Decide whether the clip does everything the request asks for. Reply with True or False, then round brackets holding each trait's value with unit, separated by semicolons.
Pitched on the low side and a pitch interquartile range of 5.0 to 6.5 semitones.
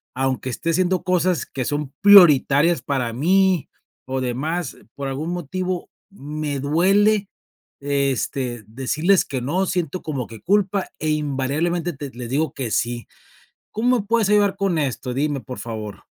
False (150 Hz; 5.6 semitones)